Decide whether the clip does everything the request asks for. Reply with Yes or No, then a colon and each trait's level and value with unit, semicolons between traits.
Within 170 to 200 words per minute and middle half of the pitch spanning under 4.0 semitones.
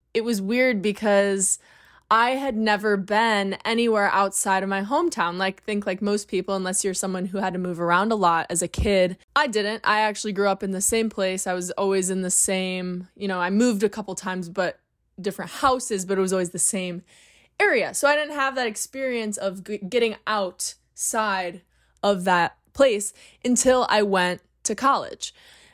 Yes: average, 190 wpm; average, 2.9 semitones